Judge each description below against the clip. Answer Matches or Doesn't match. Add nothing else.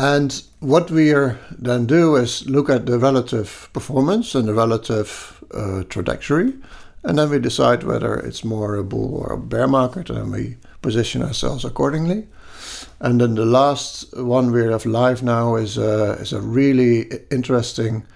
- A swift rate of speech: Doesn't match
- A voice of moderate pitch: Doesn't match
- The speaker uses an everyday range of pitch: Matches